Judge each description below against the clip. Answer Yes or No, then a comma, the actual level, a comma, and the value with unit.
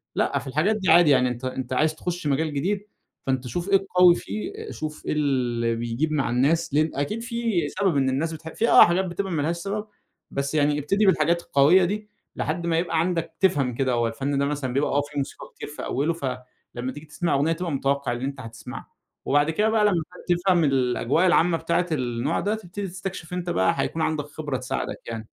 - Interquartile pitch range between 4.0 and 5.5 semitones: Yes, average, 4.6 semitones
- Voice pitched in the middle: Yes, medium, 155 Hz